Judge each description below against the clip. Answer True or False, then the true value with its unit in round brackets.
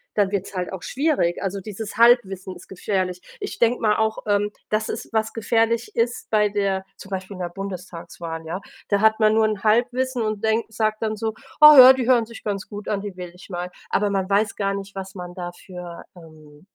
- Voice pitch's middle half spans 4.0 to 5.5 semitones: False (2.9 semitones)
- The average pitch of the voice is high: True (205 Hz)